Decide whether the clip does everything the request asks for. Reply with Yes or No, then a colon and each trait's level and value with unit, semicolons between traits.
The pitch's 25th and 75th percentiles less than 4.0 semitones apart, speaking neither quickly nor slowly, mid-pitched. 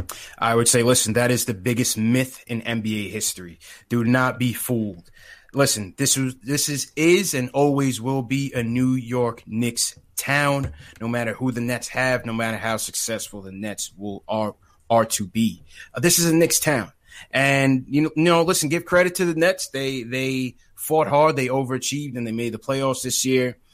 No: average, 3.2 semitones; average, 195 wpm; low, 125 Hz